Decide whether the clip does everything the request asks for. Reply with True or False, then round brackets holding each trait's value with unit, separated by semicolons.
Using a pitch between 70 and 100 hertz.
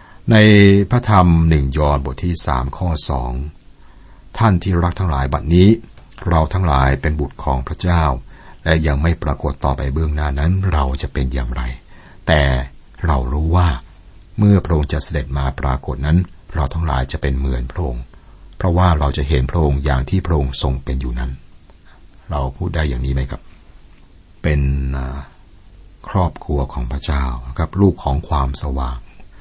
True (75 Hz)